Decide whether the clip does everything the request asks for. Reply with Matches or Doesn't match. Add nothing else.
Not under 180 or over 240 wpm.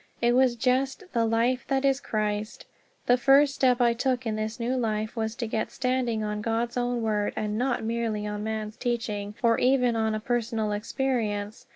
Matches